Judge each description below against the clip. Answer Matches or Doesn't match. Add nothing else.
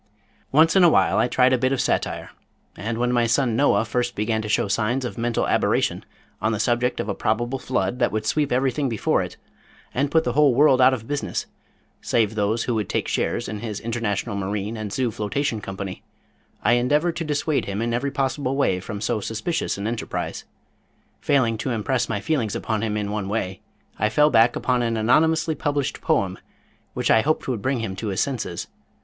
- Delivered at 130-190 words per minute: Doesn't match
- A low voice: Matches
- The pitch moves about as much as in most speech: Matches